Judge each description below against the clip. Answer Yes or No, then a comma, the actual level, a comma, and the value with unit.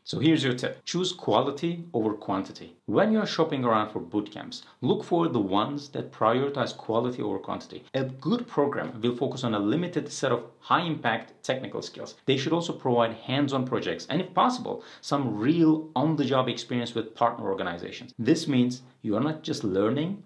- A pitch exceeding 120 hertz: Yes, medium, 140 Hz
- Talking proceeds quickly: No, average, 195 wpm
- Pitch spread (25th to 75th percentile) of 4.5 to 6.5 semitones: Yes, average, 5.0 semitones